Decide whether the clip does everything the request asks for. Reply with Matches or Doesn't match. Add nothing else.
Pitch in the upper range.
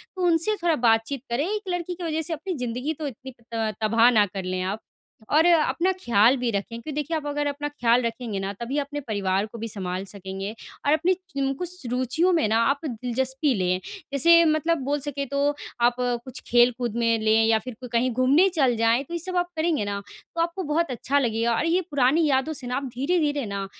Matches